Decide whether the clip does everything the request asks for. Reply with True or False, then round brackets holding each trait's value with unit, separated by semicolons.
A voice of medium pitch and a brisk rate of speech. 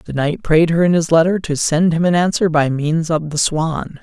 True (160 Hz; 255 wpm)